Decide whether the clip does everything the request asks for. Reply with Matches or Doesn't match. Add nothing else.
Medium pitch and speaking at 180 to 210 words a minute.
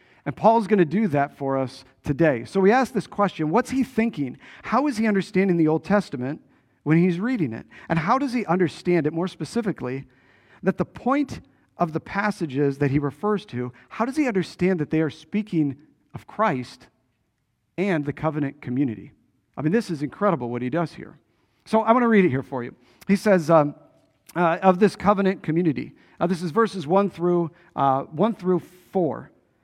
Matches